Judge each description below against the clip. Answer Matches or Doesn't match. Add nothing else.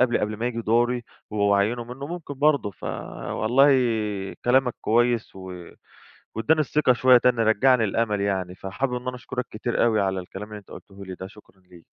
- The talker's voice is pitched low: Matches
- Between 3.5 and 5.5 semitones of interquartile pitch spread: Matches